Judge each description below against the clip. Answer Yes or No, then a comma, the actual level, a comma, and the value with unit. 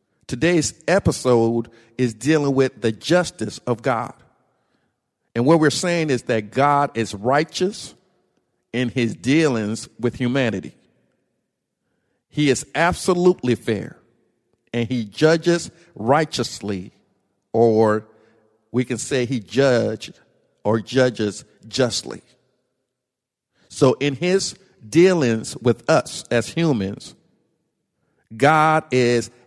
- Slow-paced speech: Yes, slow, 100 wpm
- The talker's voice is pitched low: Yes, low, 125 Hz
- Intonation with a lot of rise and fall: No, average, 4.6 semitones